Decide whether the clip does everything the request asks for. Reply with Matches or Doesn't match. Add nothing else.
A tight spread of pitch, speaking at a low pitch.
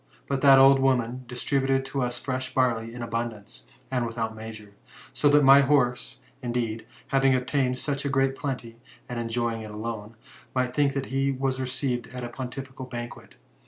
Matches